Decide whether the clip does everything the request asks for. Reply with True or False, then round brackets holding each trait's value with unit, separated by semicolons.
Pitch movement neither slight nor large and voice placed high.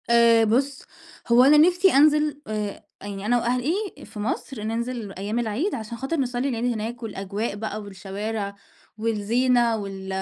True (3.3 semitones; 230 Hz)